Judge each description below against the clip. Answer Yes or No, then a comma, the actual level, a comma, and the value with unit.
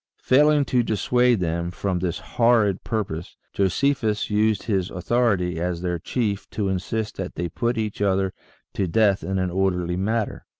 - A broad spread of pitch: No, average, 3.8 semitones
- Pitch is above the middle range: No, low, 100 Hz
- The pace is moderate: Yes, average, 160 wpm